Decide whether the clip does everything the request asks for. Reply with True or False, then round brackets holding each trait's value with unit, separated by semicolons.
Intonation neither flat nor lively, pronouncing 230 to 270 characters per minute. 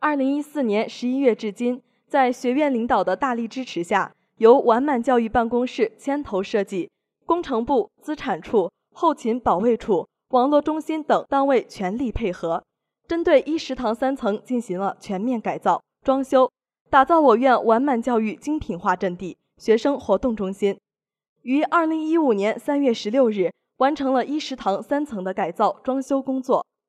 True (4.6 semitones; 260 characters per minute)